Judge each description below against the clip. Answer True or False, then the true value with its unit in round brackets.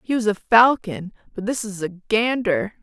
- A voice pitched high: True (210 Hz)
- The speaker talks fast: False (190 wpm)